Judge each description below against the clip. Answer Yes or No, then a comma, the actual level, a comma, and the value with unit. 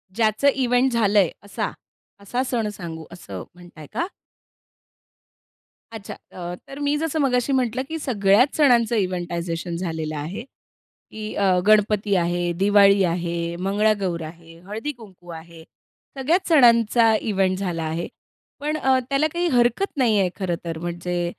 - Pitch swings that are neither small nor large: No, wide, 6.0 semitones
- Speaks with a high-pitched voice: Yes, high, 200 Hz